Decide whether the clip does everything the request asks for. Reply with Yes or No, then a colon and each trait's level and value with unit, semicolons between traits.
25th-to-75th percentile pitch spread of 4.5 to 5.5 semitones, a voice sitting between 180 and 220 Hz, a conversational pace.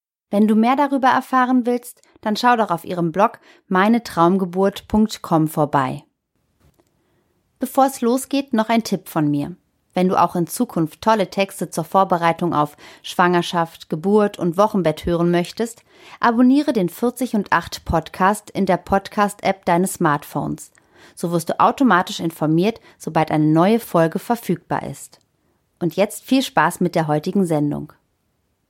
Yes: average, 4.8 semitones; high, 190 Hz; average, 145 wpm